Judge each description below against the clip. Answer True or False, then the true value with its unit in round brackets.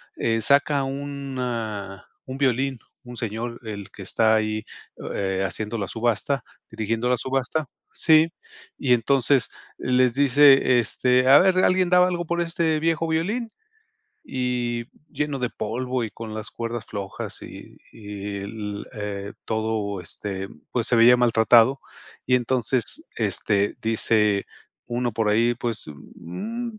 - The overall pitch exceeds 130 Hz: False (120 Hz)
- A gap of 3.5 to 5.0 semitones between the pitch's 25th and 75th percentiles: True (4.1 semitones)